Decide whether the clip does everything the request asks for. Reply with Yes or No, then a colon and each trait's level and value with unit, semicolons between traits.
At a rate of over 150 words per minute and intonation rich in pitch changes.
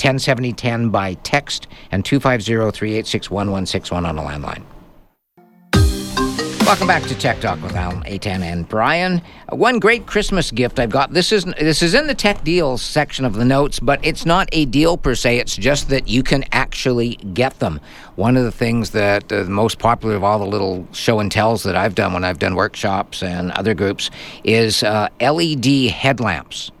Yes: average, 190 wpm; wide, 6.0 semitones